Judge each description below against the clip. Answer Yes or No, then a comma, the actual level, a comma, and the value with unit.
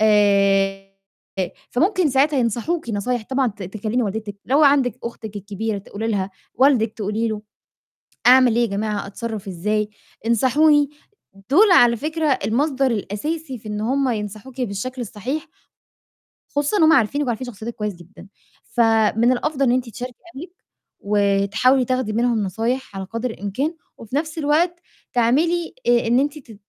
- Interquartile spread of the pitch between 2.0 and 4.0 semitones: No, average, 4.5 semitones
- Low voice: No, high, 235 Hz